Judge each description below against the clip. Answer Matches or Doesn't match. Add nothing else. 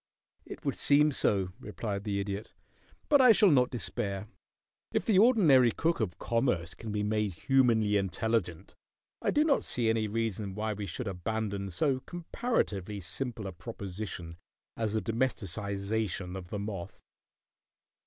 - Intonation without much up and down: Doesn't match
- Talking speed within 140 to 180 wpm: Matches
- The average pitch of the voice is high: Doesn't match